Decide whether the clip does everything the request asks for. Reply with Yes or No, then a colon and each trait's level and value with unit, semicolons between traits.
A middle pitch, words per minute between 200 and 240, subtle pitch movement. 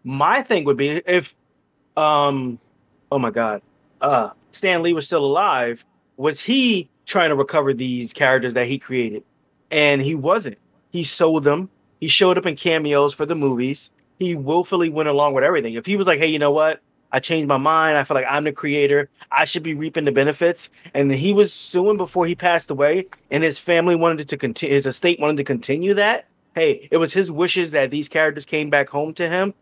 No: medium, 150 Hz; fast, 205 wpm; average, 3.5 semitones